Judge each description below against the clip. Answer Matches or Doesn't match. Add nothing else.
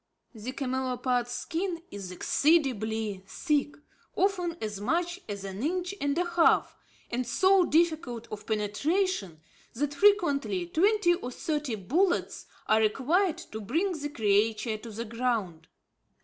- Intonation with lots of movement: Matches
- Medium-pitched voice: Doesn't match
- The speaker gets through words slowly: Matches